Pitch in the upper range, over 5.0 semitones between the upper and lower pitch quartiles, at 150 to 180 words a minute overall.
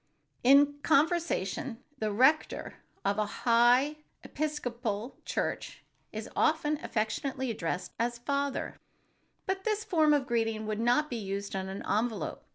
No: high, 245 Hz; wide, 5.4 semitones; slow, 135 wpm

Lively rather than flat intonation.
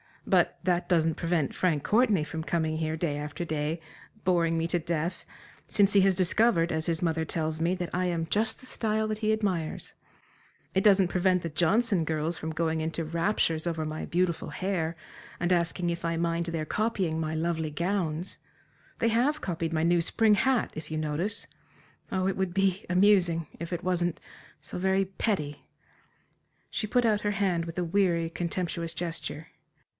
No: average, 3.0 semitones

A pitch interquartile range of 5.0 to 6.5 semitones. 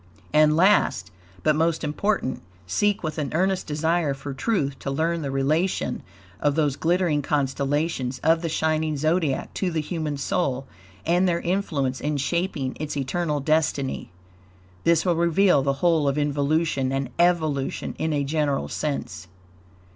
No: average, 3.4 semitones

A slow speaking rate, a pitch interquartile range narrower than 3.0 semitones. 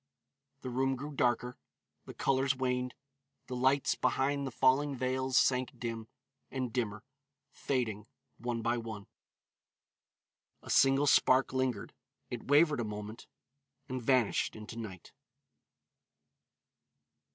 Yes: slow, 115 wpm; narrow, 2.4 semitones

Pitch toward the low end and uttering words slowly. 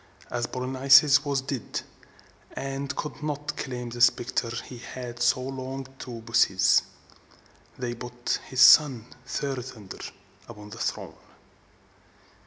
Yes: low, 125 Hz; slow, 120 wpm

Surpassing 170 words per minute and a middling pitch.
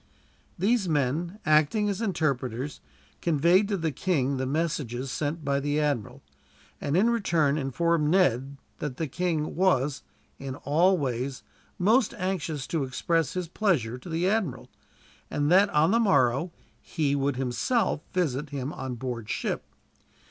No: average, 145 wpm; medium, 150 Hz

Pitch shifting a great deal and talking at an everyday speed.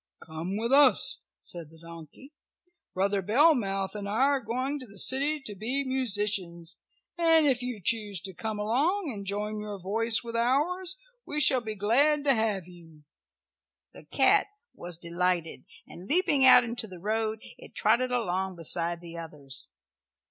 Yes: wide, 6.1 semitones; average, 160 wpm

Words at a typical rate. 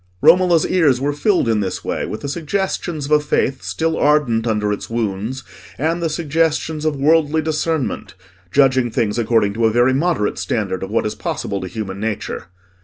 Yes: average, 180 wpm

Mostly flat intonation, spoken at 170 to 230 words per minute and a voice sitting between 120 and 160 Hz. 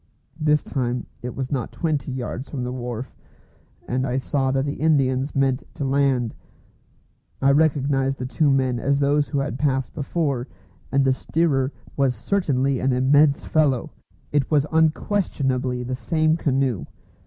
No: narrow, 2.2 semitones; average, 155 wpm; low, 135 Hz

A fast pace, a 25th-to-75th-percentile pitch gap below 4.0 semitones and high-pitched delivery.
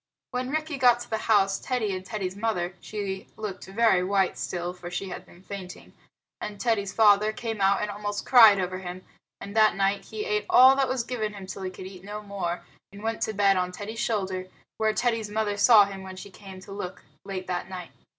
Yes: fast, 220 wpm; narrow, 2.6 semitones; high, 200 Hz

